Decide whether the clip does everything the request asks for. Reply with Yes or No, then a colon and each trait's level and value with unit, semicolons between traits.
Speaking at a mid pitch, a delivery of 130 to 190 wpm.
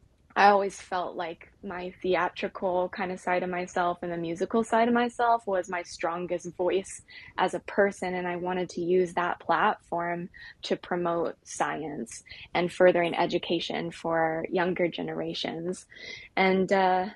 Yes: medium, 180 Hz; average, 145 wpm